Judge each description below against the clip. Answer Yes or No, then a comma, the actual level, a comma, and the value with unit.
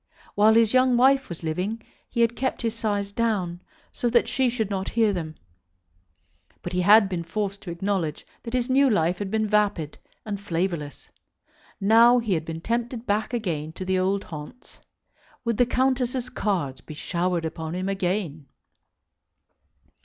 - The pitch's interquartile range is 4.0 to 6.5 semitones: Yes, average, 5.0 semitones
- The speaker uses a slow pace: No, average, 165 wpm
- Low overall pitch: No, high, 200 Hz